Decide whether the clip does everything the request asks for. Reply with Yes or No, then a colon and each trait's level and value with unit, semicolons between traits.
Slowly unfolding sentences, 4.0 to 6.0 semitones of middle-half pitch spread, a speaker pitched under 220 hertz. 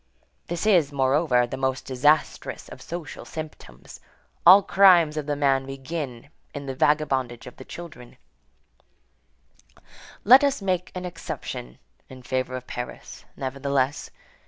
Yes: slow, 130 wpm; average, 4.4 semitones; medium, 140 Hz